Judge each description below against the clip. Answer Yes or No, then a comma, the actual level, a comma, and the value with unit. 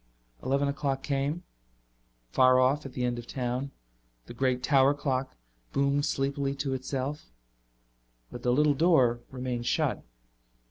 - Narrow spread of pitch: Yes, narrow, 1.8 semitones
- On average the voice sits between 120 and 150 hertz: Yes, low, 135 Hz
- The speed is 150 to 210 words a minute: No, slow, 135 wpm